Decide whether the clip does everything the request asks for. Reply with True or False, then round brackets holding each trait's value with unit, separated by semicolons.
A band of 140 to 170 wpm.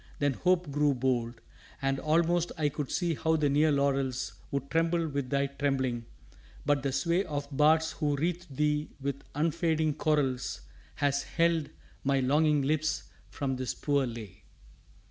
True (150 wpm)